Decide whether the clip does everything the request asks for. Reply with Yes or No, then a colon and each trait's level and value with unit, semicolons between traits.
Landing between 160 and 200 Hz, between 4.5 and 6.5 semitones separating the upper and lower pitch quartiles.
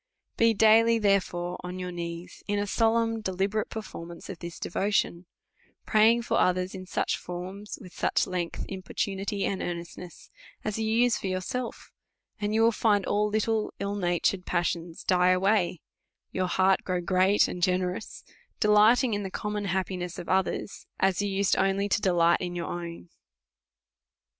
No: high, 190 Hz; average, 2.8 semitones